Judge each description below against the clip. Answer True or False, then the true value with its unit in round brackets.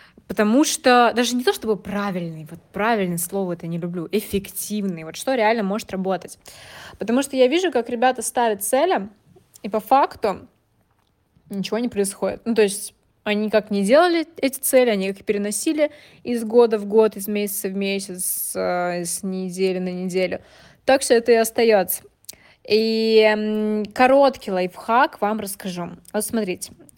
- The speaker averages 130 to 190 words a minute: True (155 wpm)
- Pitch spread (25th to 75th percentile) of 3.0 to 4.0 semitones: True (3.7 semitones)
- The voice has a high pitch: True (210 Hz)